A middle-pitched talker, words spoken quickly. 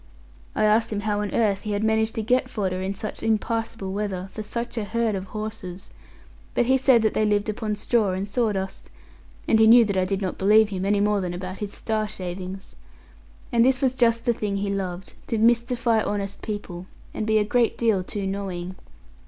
No: high, 210 Hz; fast, 210 wpm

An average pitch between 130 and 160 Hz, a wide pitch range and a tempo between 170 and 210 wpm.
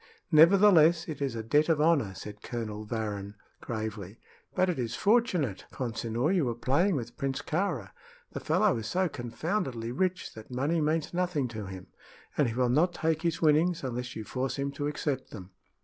Yes: low, 135 Hz; wide, 6.3 semitones; average, 180 wpm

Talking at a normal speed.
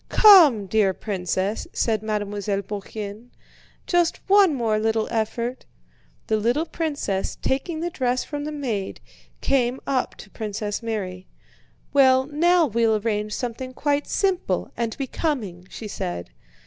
No: slow, 130 wpm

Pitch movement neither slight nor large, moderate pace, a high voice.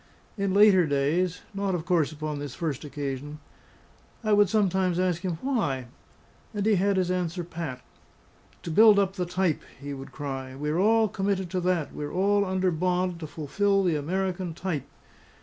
No: average, 4.1 semitones; average, 170 wpm; medium, 180 Hz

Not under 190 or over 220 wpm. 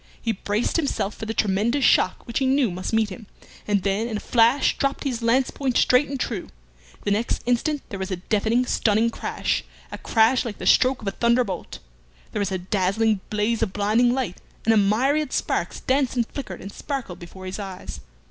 Yes: fast, 205 wpm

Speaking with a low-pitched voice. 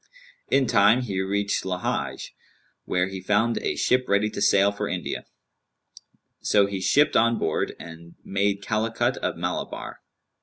Yes: low, 100 Hz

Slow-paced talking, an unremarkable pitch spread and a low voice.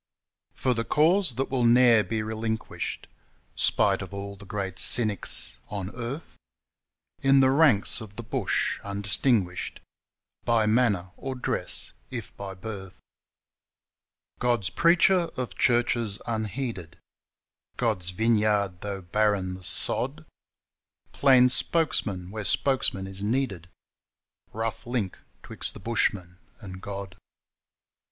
Yes: slow, 115 wpm; average, 4.0 semitones; low, 110 Hz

